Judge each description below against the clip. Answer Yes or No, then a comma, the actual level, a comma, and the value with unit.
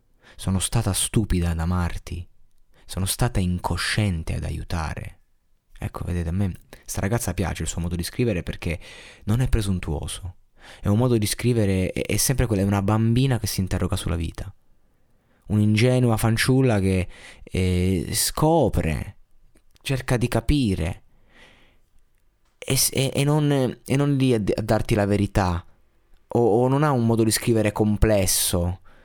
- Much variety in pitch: No, average, 4.5 semitones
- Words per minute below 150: No, average, 155 wpm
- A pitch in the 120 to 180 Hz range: No, low, 100 Hz